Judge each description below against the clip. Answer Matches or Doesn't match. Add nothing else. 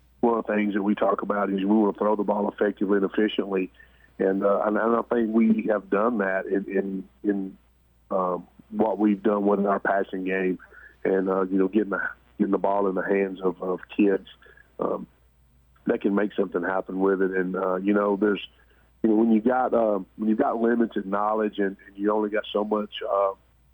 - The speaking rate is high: Matches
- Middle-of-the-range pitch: Doesn't match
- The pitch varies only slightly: Matches